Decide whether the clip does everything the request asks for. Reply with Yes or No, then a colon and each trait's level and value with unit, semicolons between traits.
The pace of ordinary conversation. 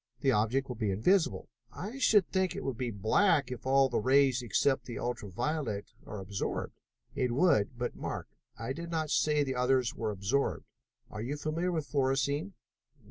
Yes: average, 180 wpm